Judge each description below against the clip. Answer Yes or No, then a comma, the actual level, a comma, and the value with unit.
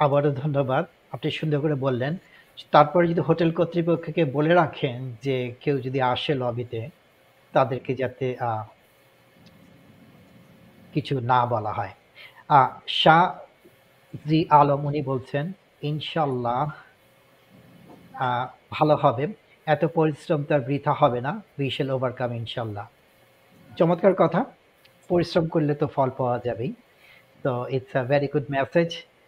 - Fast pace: No, average, 110 wpm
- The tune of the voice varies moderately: Yes, average, 3.5 semitones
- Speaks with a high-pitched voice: No, medium, 145 Hz